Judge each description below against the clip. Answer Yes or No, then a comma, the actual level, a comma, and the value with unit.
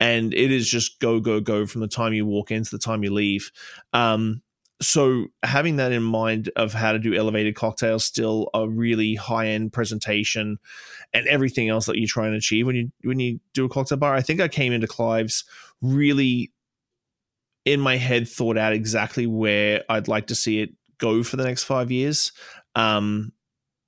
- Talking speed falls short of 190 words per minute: No, average, 195 wpm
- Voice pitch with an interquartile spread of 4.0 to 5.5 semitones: No, narrow, 2.6 semitones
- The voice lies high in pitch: No, low, 115 Hz